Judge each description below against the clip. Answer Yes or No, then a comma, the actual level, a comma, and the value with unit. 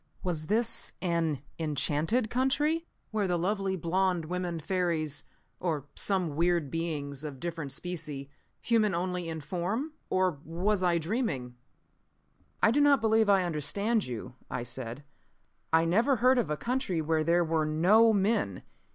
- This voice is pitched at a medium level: Yes, medium, 175 Hz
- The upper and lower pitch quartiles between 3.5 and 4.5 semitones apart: No, average, 5.3 semitones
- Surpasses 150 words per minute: No, average, 145 wpm